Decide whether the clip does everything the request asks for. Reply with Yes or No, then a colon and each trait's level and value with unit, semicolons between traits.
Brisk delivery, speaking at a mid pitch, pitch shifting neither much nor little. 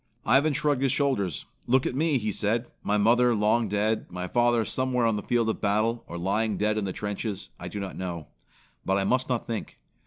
No: fast, 215 wpm; low, 110 Hz; average, 3.3 semitones